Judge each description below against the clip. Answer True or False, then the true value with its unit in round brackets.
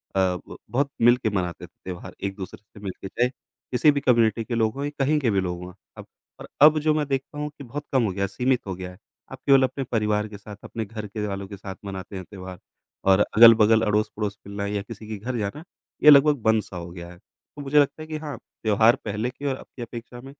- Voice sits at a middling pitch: False (110 Hz)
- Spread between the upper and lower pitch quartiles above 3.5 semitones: True (5.2 semitones)